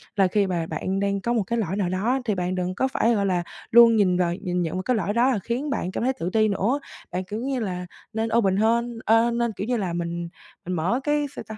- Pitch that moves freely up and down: No, average, 4.4 semitones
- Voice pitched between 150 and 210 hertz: Yes, high, 205 Hz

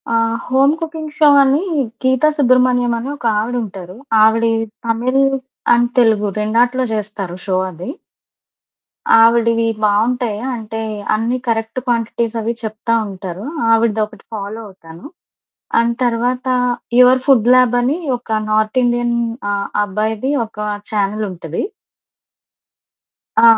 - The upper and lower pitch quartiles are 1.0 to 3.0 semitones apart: Yes, narrow, 2.6 semitones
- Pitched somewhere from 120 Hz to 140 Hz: No, high, 230 Hz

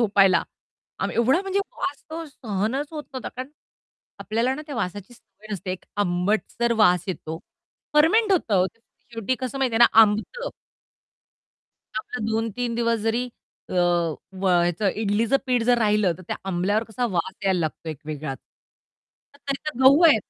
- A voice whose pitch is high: Yes, high, 220 Hz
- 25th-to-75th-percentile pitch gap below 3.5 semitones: No, average, 5.2 semitones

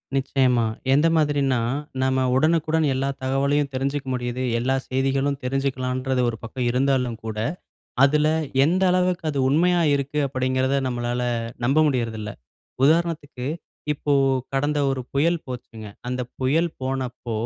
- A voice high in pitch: No, low, 135 Hz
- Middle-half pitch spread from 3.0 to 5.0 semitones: No, narrow, 2.5 semitones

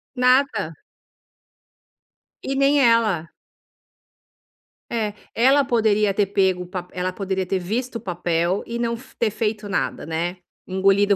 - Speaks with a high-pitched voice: Yes, high, 205 Hz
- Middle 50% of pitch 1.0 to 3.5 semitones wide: No, average, 4.1 semitones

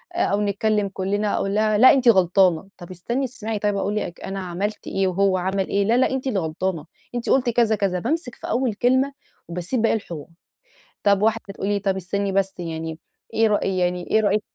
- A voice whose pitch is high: Yes, high, 200 Hz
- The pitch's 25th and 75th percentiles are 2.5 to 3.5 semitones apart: Yes, average, 3.0 semitones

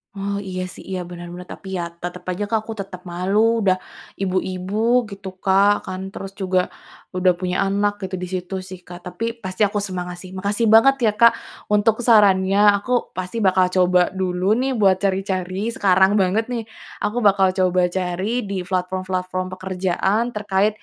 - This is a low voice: No, high, 190 Hz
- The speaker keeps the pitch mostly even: Yes, narrow, 1.6 semitones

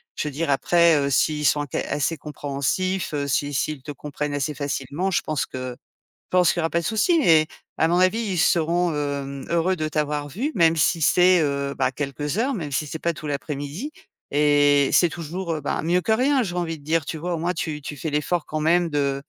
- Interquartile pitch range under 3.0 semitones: No, average, 3.4 semitones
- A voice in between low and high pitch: Yes, medium, 155 Hz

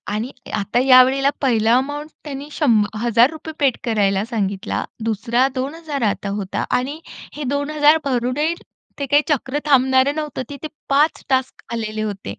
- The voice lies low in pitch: No, very high, 260 Hz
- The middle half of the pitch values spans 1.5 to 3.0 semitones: No, average, 4.2 semitones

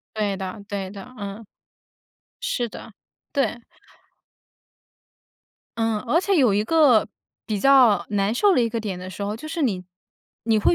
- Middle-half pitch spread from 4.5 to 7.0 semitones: Yes, average, 4.8 semitones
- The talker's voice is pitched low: No, high, 220 Hz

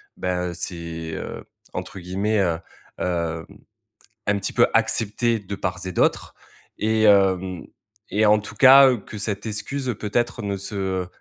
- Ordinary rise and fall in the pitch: Yes, average, 3.0 semitones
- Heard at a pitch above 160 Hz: No, low, 100 Hz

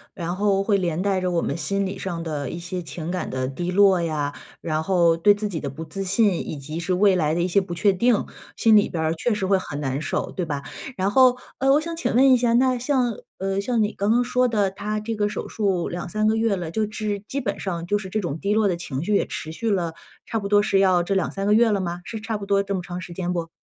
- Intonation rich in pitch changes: No, average, 3.7 semitones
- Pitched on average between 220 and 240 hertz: No, high, 195 Hz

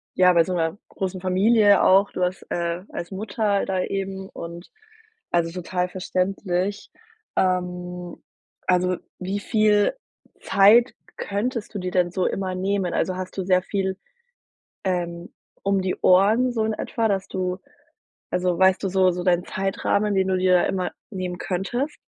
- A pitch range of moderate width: No, narrow, 1.7 semitones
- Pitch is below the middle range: No, medium, 185 Hz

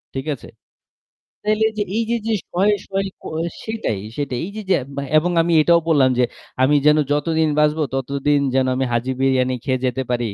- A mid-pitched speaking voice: Yes, medium, 145 Hz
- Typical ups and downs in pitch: Yes, average, 4.8 semitones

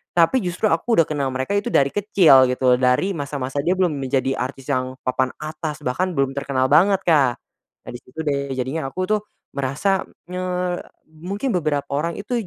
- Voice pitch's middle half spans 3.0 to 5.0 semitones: No, wide, 5.4 semitones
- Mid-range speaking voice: Yes, medium, 145 Hz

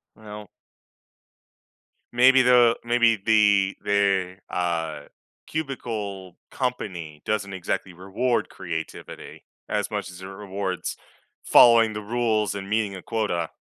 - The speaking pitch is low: Yes, low, 100 Hz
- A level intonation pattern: No, average, 3.3 semitones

